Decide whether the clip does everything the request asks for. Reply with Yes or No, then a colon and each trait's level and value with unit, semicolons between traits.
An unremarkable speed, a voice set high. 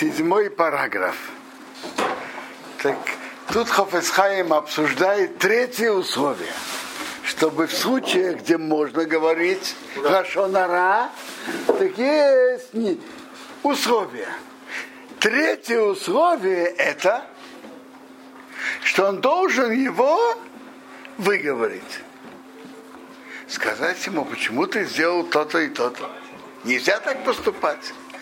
No: slow, 80 wpm; high, 230 Hz